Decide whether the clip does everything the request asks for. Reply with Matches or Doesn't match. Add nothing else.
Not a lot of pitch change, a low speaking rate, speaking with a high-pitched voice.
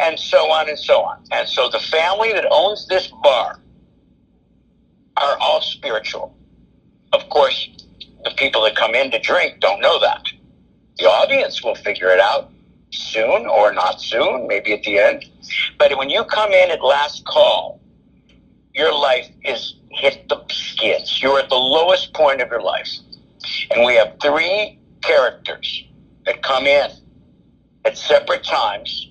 Doesn't match